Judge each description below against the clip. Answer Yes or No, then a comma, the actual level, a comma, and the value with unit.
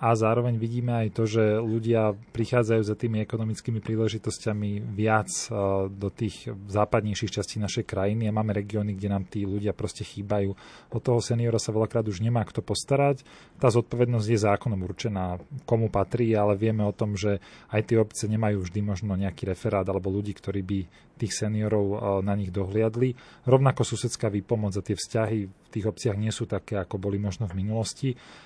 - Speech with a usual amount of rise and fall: No, narrow, 2.2 semitones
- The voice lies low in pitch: Yes, low, 110 Hz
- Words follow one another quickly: Yes, fast, 175 wpm